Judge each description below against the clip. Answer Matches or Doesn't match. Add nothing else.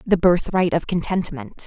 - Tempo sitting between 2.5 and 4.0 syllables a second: Doesn't match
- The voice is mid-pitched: Matches